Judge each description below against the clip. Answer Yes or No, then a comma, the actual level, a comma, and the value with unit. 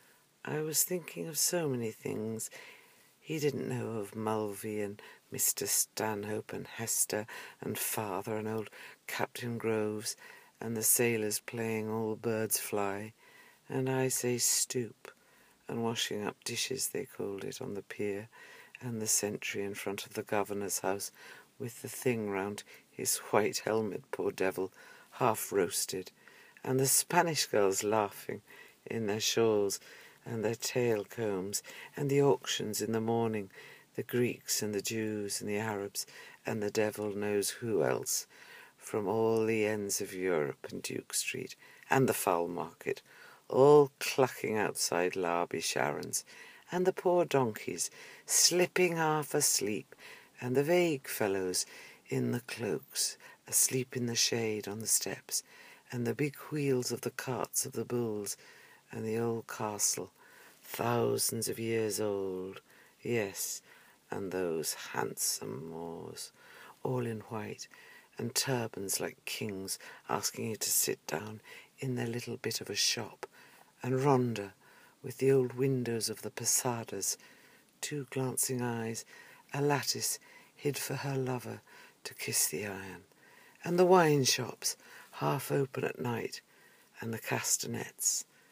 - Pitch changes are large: No, average, 4.0 semitones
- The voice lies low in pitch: Yes, low, 115 Hz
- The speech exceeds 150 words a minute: No, average, 140 wpm